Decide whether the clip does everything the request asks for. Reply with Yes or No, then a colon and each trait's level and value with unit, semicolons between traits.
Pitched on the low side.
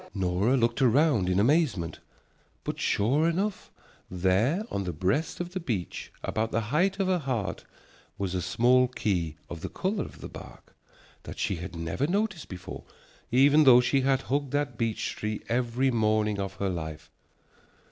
Yes: low, 115 Hz